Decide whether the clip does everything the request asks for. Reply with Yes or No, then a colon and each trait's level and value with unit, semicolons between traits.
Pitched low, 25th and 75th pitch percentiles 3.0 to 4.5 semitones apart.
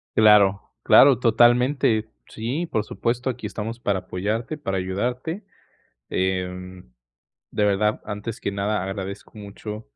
Yes: low, 105 Hz; average, 3.4 semitones